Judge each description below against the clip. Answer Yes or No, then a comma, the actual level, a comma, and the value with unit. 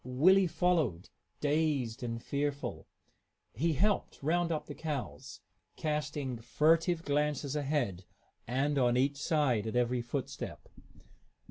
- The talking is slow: Yes, slow, 115 wpm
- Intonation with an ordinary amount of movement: Yes, average, 4.1 semitones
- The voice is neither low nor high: Yes, medium, 145 Hz